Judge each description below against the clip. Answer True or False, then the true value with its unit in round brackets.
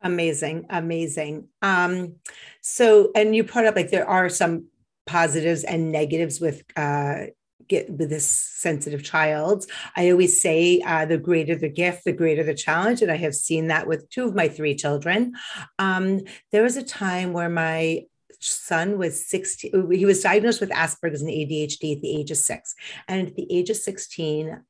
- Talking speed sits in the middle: True (175 wpm)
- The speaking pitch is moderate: True (170 Hz)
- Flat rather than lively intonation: False (3.7 semitones)